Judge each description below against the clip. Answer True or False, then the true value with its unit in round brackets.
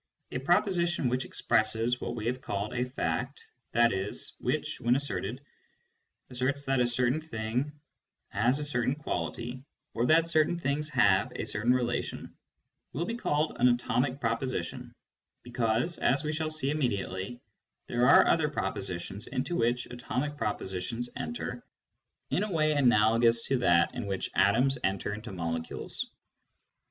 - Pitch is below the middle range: True (125 Hz)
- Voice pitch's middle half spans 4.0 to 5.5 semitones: True (4.4 semitones)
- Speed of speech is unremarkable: True (145 wpm)